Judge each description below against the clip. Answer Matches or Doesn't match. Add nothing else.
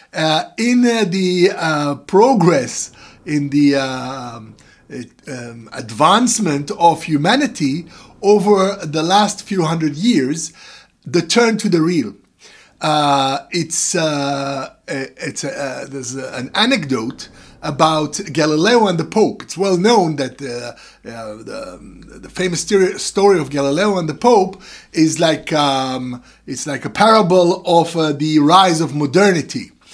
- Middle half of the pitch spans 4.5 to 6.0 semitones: Matches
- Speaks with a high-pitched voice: Doesn't match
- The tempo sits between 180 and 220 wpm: Doesn't match